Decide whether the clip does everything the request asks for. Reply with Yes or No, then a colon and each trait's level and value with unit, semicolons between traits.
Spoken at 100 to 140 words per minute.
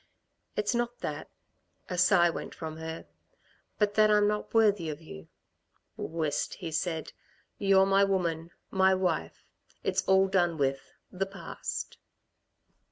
Yes: slow, 135 wpm